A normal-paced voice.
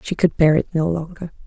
No: fast, 245 wpm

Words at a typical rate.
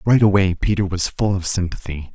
Yes: average, 195 wpm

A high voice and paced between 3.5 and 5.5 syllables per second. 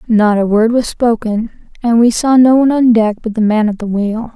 Yes: high, 225 Hz; 5.2 syllables/s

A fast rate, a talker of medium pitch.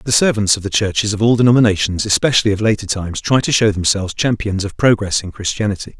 No: fast, 210 wpm; low, 105 Hz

